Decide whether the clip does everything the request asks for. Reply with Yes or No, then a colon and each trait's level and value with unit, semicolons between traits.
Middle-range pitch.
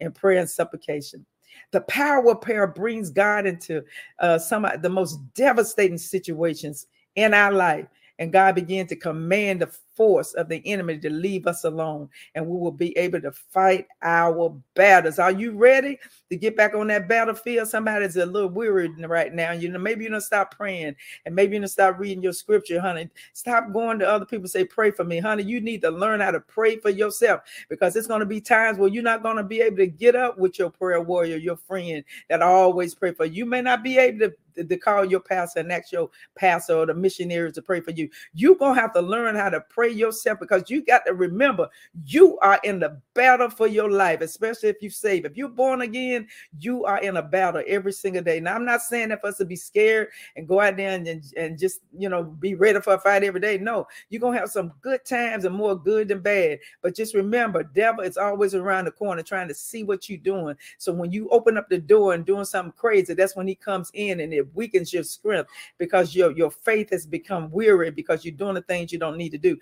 No: high, 195 Hz